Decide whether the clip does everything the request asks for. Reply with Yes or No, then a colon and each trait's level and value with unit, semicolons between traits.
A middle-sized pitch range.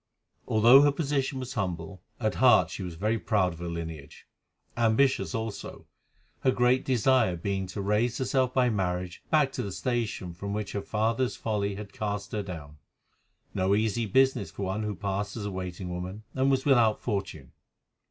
Yes: average, 4.6 semitones